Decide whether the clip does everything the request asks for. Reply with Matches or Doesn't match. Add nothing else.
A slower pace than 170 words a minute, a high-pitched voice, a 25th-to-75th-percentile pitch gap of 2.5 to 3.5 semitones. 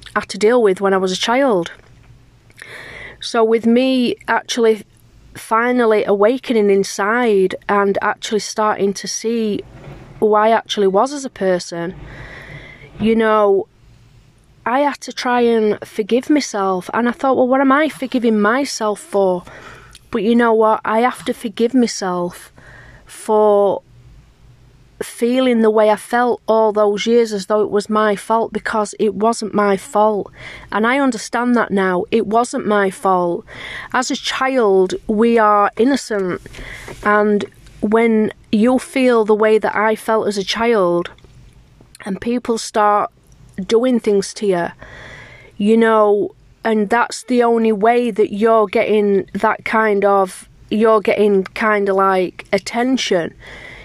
Matches